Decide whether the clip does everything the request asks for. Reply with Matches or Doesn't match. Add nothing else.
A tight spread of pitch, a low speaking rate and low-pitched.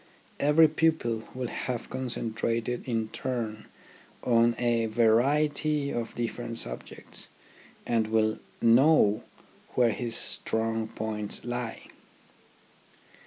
Matches